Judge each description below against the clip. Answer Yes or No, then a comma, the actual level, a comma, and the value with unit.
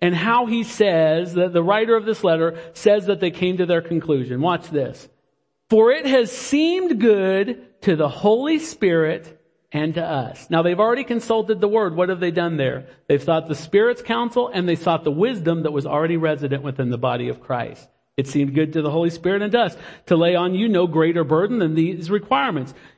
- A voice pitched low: No, medium, 175 Hz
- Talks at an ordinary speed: No, fast, 210 wpm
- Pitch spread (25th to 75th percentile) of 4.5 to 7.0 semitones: Yes, wide, 5.4 semitones